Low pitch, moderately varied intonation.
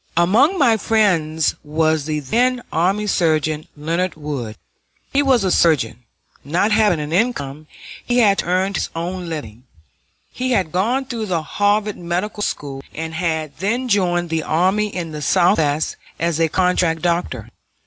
No: medium, 175 Hz; average, 5.0 semitones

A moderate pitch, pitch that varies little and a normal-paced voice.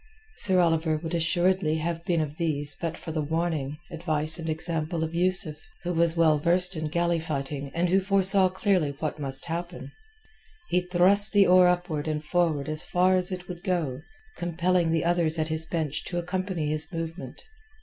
Yes: medium, 170 Hz; narrow, 2.3 semitones; average, 180 wpm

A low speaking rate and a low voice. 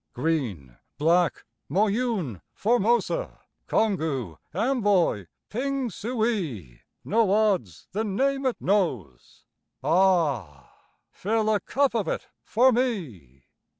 No: slow, 90 wpm; high, 195 Hz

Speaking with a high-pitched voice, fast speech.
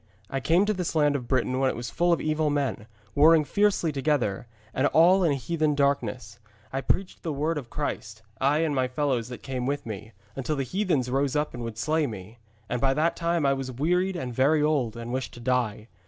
No: medium, 140 Hz; fast, 220 wpm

